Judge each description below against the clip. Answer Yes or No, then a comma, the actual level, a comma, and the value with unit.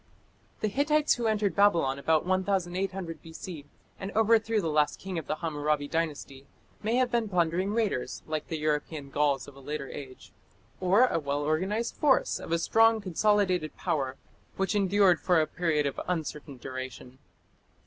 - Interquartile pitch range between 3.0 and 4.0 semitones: No, wide, 5.4 semitones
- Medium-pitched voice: Yes, medium, 170 Hz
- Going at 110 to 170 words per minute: Yes, average, 160 wpm